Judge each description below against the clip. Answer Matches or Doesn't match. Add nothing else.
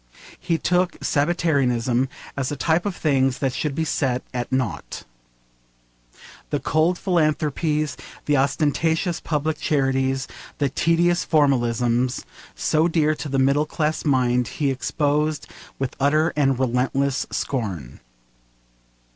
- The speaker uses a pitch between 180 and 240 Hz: Doesn't match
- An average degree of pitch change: Matches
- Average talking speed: Doesn't match